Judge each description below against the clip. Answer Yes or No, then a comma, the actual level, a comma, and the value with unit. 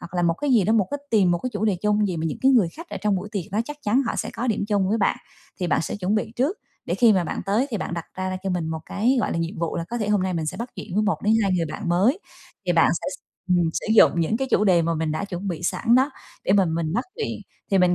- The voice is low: No, high, 195 Hz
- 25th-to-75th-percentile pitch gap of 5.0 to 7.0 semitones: No, average, 4.3 semitones